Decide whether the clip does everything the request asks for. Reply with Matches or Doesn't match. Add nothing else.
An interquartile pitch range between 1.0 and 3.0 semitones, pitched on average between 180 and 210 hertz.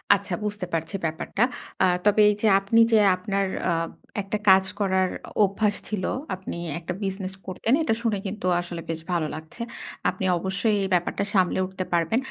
Matches